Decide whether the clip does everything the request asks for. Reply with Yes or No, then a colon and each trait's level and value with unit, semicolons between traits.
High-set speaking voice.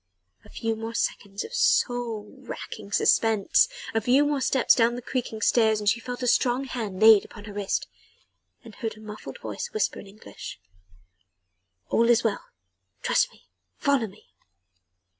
Yes: high, 225 Hz